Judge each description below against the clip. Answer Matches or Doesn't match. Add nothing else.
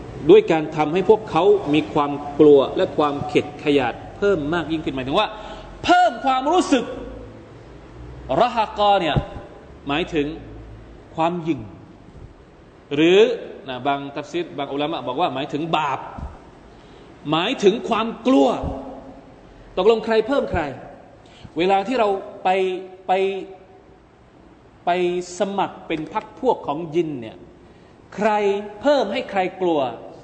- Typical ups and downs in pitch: Doesn't match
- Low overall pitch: Doesn't match